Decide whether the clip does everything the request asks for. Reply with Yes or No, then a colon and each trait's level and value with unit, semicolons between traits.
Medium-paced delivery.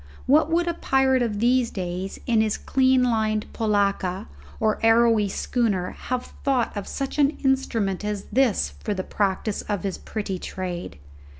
Yes: average, 160 wpm